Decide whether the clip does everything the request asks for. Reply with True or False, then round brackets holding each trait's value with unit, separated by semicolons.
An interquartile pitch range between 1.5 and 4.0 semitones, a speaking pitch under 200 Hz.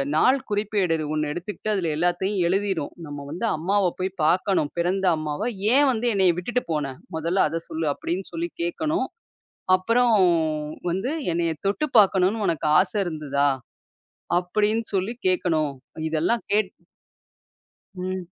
False (4.4 semitones; 185 Hz)